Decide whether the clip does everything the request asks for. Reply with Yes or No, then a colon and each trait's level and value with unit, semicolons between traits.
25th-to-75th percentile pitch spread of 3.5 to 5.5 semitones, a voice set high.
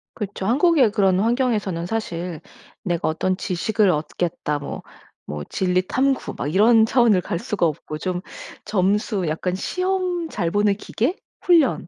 Yes: average, 5.2 semitones; high, 200 Hz